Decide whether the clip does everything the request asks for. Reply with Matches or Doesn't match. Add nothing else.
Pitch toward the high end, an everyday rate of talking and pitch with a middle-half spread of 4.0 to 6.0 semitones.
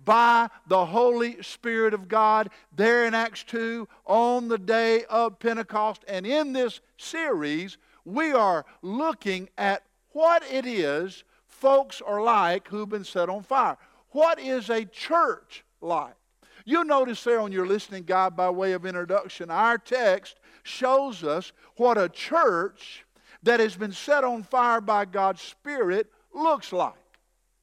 Matches